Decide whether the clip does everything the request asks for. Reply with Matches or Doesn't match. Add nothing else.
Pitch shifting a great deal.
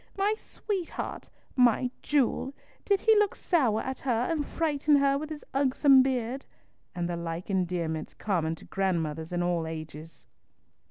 Matches